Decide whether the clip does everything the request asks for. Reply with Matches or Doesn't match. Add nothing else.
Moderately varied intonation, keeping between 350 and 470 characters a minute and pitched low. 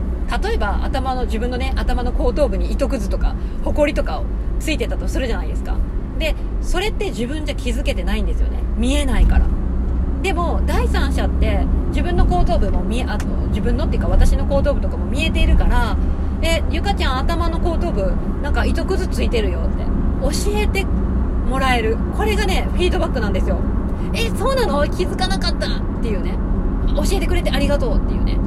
Matches